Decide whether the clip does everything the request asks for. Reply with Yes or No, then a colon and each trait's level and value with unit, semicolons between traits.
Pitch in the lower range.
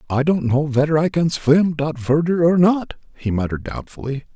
No: medium, 150 Hz